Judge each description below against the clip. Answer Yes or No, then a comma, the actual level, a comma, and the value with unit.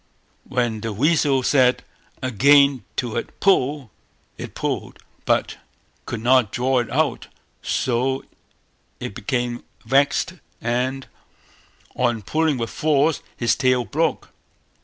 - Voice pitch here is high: No, low, 130 Hz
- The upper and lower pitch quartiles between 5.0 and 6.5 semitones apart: No, average, 2.8 semitones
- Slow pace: Yes, slow, 115 wpm